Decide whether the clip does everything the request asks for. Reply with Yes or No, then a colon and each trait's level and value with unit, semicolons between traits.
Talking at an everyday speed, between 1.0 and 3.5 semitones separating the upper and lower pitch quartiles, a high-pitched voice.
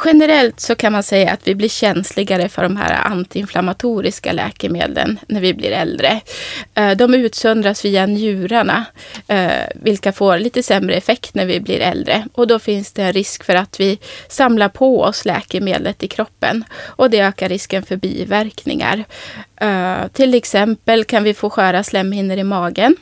Yes: average, 160 wpm; average, 2.9 semitones; high, 205 Hz